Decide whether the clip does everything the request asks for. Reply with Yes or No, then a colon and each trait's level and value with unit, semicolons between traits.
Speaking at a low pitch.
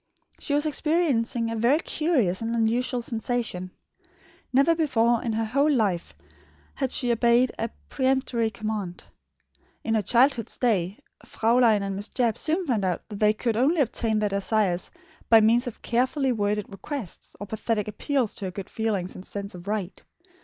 No: high, 230 Hz